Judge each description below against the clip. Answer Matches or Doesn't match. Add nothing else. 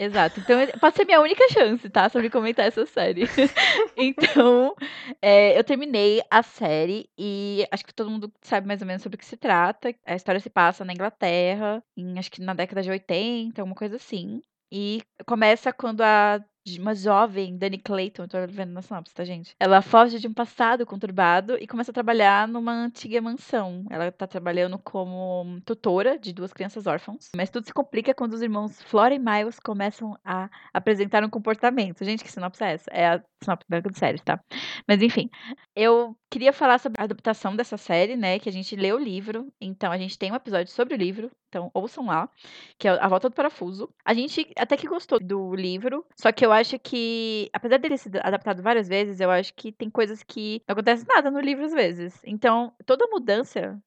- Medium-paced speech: Doesn't match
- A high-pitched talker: Matches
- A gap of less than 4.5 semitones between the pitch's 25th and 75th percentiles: Matches